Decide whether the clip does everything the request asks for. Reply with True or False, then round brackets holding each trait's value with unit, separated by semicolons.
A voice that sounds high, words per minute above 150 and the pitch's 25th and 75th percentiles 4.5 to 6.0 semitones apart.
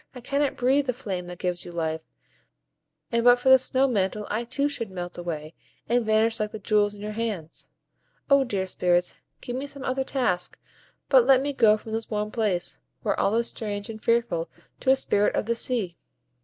True (220 Hz; 205 wpm; 5.0 semitones)